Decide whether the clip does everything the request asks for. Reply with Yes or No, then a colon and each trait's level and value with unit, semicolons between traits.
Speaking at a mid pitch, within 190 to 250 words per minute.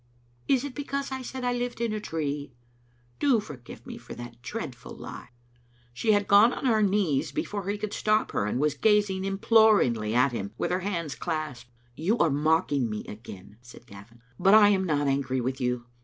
Yes: medium, 160 Hz; average, 195 wpm